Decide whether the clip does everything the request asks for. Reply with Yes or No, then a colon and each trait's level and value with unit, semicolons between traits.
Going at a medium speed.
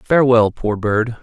Yes: average, 145 wpm